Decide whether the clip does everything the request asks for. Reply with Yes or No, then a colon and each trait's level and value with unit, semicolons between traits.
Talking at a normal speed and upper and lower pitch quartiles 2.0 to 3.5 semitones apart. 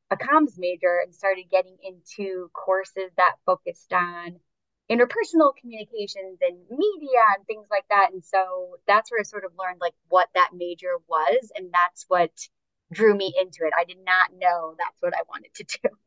No: average, 185 wpm; average, 4.3 semitones